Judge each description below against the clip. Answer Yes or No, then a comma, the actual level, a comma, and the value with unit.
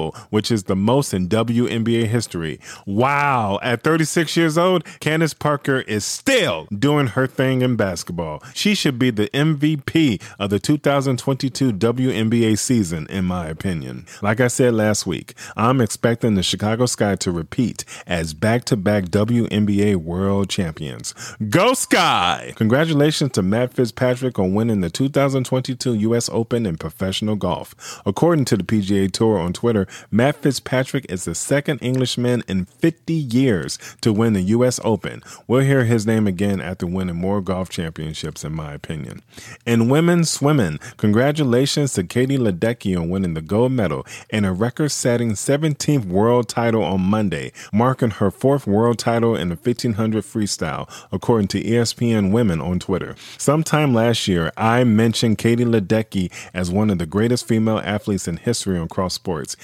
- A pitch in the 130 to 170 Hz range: No, low, 115 Hz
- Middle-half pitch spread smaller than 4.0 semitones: No, average, 4.6 semitones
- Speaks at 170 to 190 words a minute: No, average, 155 wpm